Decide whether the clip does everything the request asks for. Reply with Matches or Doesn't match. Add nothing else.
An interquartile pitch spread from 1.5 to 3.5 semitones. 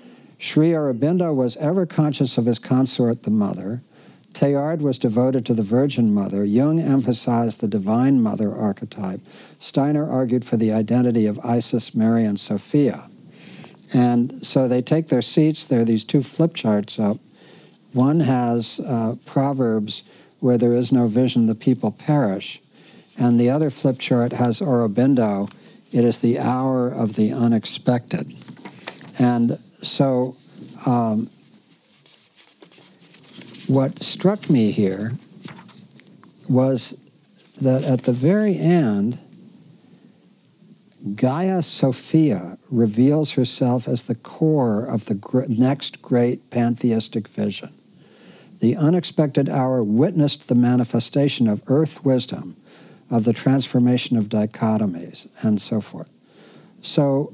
Doesn't match